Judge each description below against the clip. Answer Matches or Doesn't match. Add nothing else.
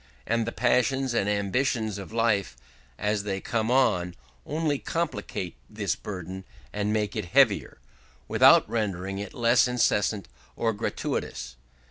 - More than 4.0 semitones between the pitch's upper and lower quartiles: Doesn't match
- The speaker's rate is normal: Doesn't match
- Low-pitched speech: Matches